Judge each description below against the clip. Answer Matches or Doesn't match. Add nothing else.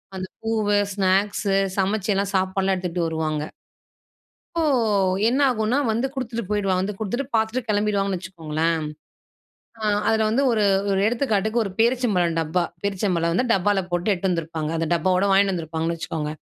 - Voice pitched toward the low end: Doesn't match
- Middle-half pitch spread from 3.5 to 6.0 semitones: Matches